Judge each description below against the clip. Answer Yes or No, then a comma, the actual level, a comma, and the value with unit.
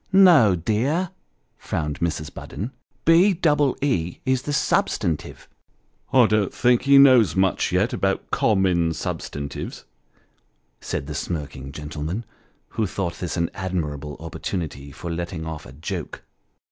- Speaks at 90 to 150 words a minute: Yes, average, 140 wpm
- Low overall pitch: Yes, very low, 90 Hz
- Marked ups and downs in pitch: Yes, wide, 8.2 semitones